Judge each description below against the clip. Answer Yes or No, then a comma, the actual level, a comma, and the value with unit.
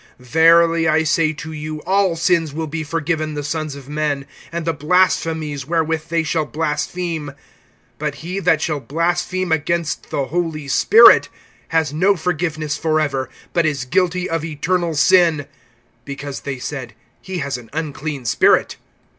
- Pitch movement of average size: No, narrow, 2.3 semitones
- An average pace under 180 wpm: Yes, average, 150 wpm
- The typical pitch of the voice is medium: Yes, medium, 155 Hz